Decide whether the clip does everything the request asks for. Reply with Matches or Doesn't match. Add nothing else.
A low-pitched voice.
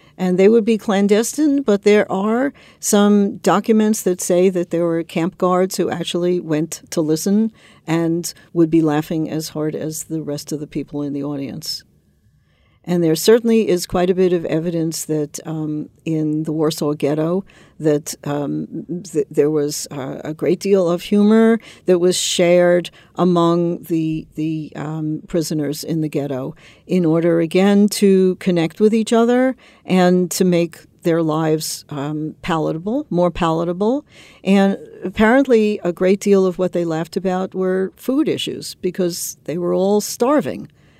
Doesn't match